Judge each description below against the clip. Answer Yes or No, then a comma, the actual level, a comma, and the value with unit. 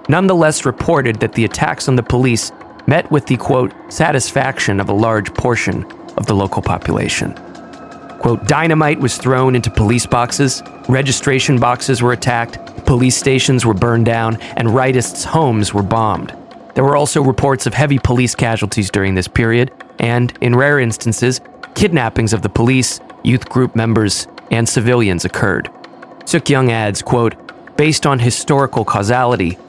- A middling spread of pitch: Yes, average, 3.0 semitones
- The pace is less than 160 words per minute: Yes, average, 150 wpm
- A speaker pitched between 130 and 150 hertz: No, low, 120 Hz